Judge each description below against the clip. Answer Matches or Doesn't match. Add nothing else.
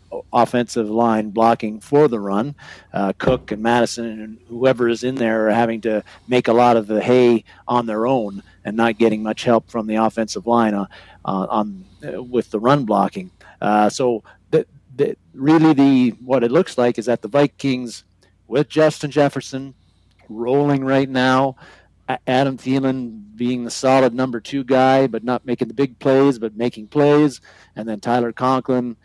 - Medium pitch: Doesn't match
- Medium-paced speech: Matches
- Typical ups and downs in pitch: Matches